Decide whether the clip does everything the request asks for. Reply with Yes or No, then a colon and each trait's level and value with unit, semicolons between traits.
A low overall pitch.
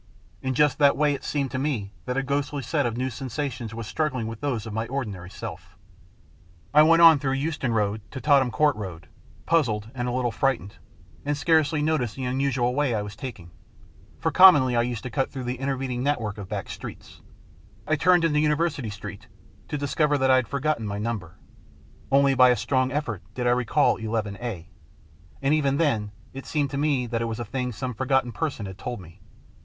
Yes: low, 130 Hz